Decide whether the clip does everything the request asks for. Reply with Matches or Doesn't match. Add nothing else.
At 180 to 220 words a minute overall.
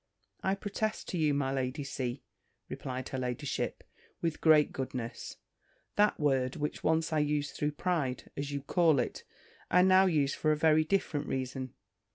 Doesn't match